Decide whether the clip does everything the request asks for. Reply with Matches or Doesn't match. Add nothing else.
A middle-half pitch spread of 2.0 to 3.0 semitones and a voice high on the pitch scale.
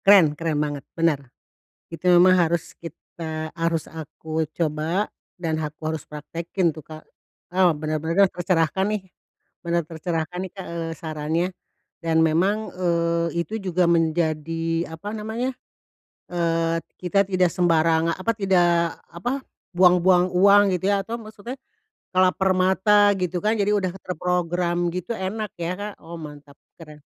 Doesn't match